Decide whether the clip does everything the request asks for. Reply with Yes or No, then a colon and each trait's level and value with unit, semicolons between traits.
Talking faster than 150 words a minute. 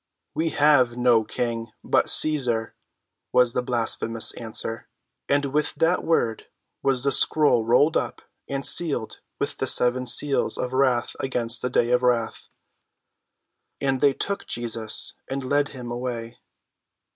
No: average, 140 wpm